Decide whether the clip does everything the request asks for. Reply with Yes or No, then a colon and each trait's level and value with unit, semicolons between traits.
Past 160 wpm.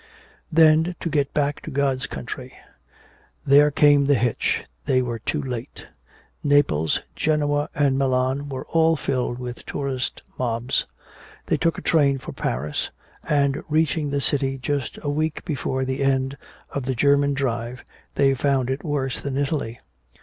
No: average, 150 wpm